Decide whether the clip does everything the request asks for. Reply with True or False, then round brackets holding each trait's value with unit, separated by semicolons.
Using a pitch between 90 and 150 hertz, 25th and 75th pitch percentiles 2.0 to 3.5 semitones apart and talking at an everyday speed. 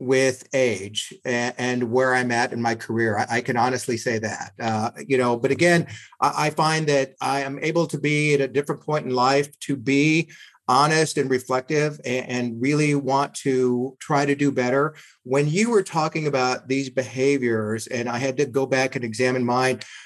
True (135 Hz; 2.7 semitones; 185 wpm)